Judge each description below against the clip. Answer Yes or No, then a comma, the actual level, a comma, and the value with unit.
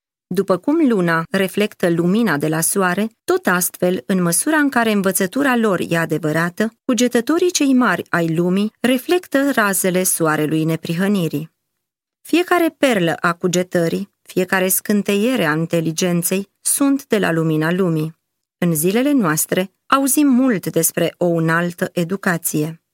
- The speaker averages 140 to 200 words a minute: No, average, 130 wpm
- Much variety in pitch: Yes, wide, 5.7 semitones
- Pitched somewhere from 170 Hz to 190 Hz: Yes, medium, 185 Hz